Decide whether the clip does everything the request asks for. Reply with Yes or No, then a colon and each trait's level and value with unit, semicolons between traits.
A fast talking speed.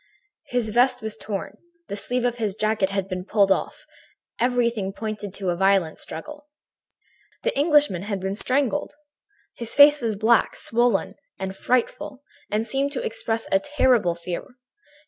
No: average, 150 wpm